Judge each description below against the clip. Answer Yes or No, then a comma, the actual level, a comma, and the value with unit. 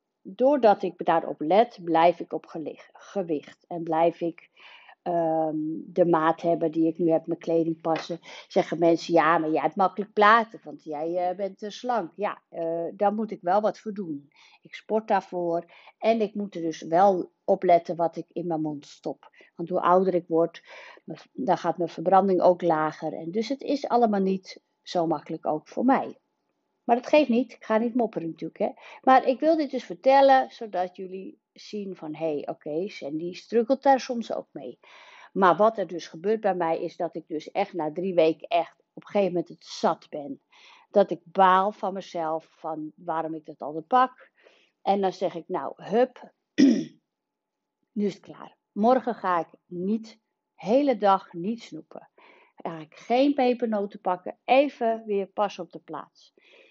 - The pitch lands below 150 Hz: No, medium, 185 Hz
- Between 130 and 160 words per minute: No, average, 190 wpm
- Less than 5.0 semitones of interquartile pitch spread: No, average, 5.3 semitones